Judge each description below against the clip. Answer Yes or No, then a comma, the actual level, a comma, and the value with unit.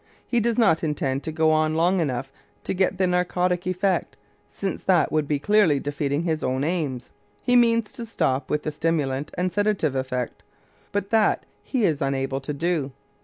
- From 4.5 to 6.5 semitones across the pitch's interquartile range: Yes, average, 5.2 semitones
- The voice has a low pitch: No, medium, 160 Hz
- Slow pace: No, average, 180 wpm